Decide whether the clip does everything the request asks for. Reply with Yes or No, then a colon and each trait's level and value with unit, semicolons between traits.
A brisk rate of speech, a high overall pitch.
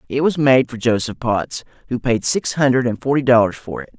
No: fast, 225 wpm; low, 125 Hz